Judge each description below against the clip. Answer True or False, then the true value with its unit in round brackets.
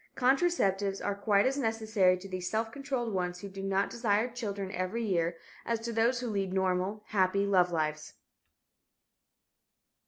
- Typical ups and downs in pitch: True (3.5 semitones)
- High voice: True (200 Hz)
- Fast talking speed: False (155 wpm)